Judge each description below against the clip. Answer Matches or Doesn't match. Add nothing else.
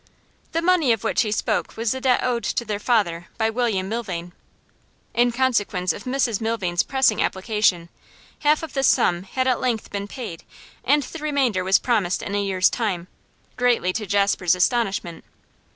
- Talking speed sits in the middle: Matches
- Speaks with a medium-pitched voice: Doesn't match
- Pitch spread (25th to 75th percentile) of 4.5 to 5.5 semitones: Matches